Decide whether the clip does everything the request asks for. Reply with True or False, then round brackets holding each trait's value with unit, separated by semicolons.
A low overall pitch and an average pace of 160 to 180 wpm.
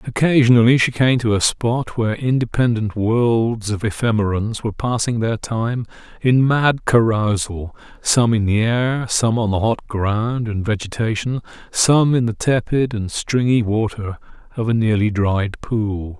False (115 Hz; 150 wpm)